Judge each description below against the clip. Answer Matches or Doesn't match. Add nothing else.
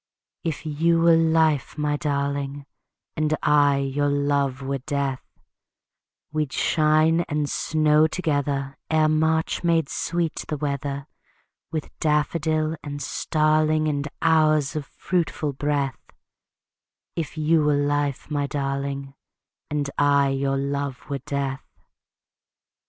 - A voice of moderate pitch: Matches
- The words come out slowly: Matches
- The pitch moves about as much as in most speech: Doesn't match